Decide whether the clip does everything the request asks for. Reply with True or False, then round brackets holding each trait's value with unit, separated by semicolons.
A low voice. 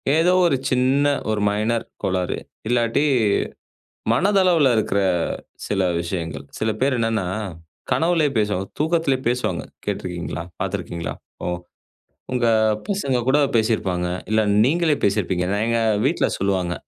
True (115 Hz)